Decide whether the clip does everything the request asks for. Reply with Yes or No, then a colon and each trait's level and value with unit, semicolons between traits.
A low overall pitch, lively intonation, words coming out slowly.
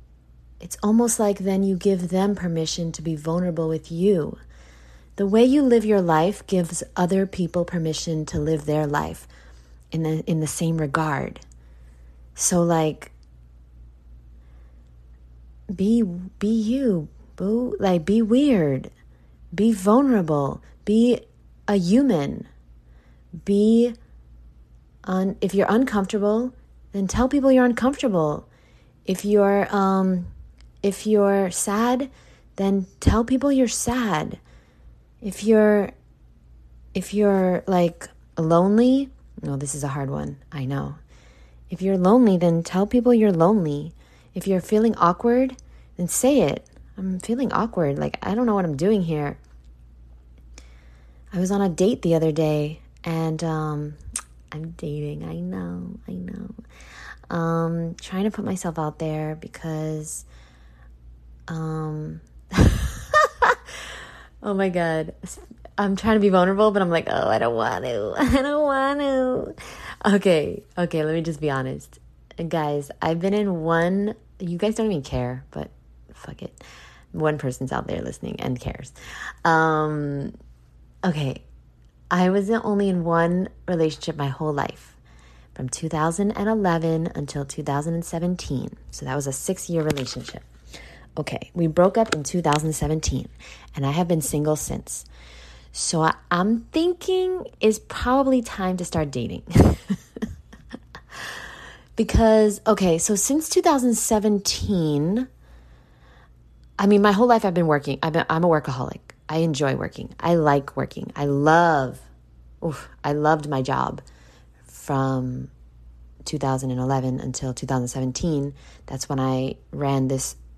No: medium, 165 Hz; wide, 8.1 semitones; slow, 130 wpm